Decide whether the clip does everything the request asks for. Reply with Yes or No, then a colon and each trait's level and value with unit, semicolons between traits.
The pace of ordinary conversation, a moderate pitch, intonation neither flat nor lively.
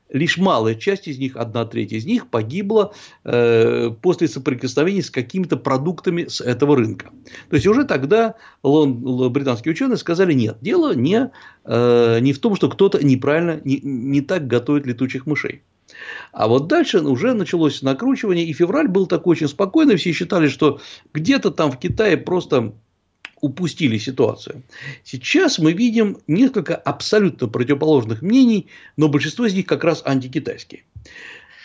No: average, 150 wpm; medium, 155 Hz; wide, 5.9 semitones